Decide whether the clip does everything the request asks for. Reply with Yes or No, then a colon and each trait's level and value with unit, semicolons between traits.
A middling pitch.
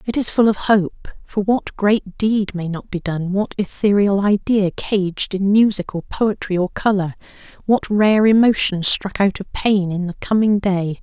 No: high, 200 Hz